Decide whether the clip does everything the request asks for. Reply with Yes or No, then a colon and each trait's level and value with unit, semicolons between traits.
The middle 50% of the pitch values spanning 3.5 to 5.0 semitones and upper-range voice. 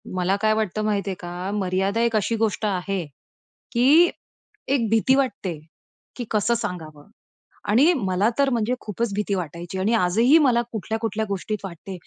Yes: average, 3.8 semitones; high, 210 Hz